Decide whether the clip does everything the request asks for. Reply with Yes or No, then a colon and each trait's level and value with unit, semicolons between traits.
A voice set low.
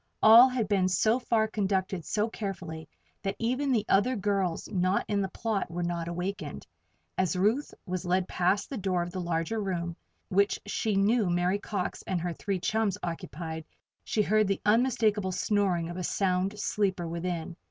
No: high, 195 Hz